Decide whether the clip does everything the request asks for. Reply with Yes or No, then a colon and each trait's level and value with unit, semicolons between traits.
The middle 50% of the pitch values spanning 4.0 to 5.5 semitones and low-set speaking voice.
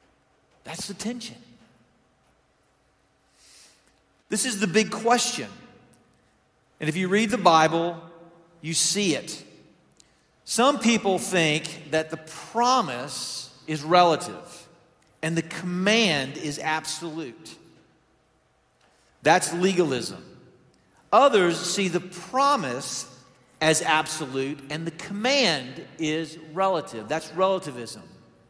No: average, 4.3 semitones; medium, 170 Hz